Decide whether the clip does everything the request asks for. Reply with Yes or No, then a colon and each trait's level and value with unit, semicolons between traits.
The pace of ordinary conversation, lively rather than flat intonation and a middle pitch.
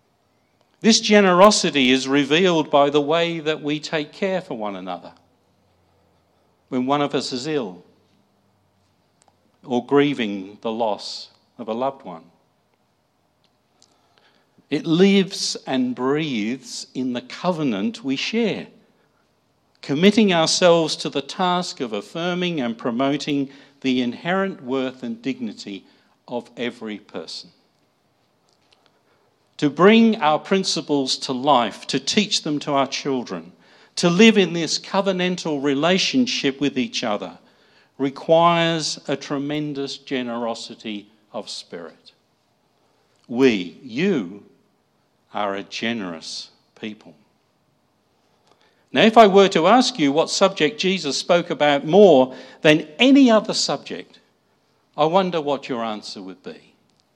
No: slow, 115 wpm; wide, 6.7 semitones; medium, 145 Hz